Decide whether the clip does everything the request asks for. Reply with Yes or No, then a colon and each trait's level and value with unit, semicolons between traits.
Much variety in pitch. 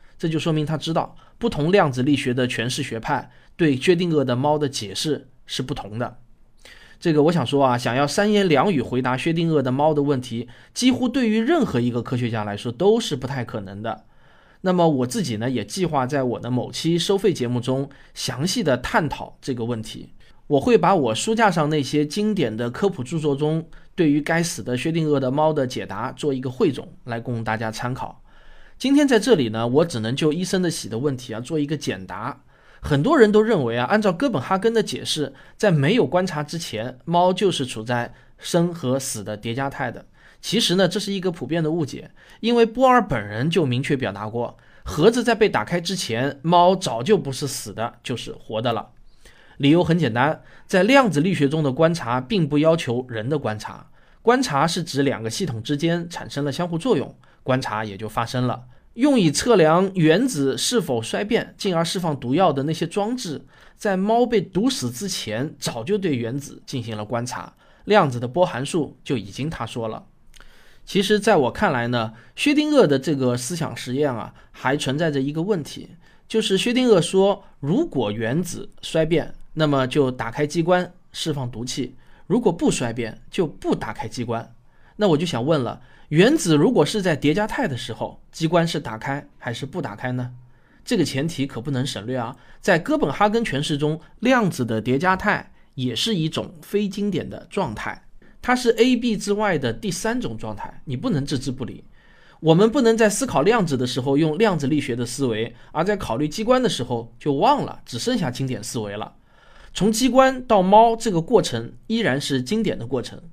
Yes: wide, 6.8 semitones